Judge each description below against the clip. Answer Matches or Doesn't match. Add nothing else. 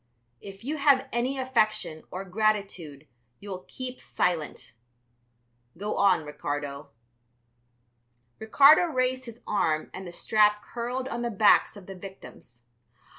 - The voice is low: Doesn't match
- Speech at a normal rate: Doesn't match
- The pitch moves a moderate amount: Doesn't match